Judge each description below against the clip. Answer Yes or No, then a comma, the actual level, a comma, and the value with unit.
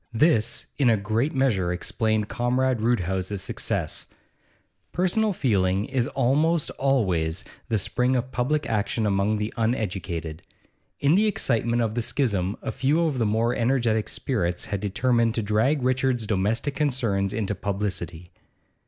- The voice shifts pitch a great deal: No, average, 4.6 semitones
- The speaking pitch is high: No, low, 115 Hz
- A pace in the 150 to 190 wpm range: No, average, 140 wpm